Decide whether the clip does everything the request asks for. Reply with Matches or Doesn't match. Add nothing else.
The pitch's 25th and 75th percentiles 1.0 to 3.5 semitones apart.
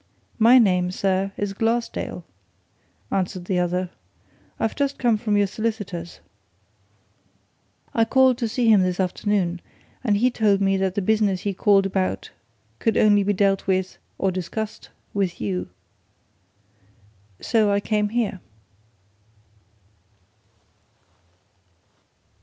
Matches